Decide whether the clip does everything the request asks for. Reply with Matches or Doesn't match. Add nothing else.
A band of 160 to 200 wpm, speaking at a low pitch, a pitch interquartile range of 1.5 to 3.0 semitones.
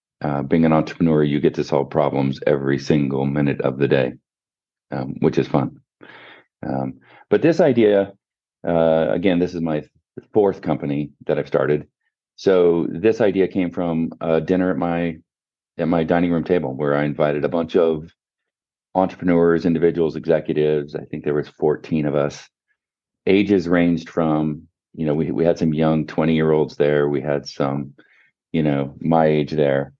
Matches